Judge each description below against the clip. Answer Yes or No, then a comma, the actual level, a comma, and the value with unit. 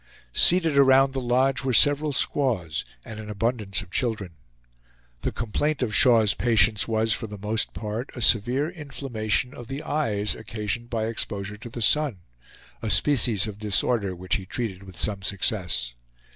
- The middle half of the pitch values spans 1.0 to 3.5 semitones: No, average, 4.1 semitones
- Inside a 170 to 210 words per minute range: No, average, 160 wpm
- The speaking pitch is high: No, low, 110 Hz